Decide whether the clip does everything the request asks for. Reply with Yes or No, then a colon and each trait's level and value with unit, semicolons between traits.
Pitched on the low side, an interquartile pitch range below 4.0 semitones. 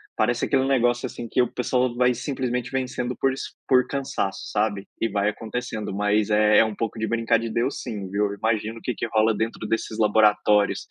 Yes: low, 115 Hz; average, 2.8 semitones